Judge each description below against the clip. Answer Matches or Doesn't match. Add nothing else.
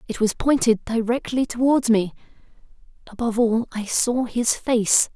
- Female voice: Matches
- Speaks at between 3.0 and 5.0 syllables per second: Matches